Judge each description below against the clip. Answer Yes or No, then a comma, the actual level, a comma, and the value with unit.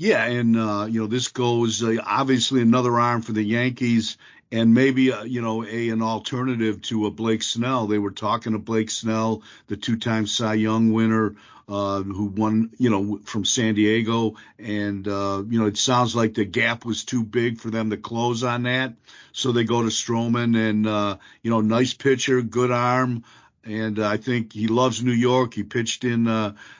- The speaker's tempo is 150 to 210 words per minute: Yes, average, 195 wpm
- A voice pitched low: Yes, low, 115 Hz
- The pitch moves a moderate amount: No, narrow, 1.8 semitones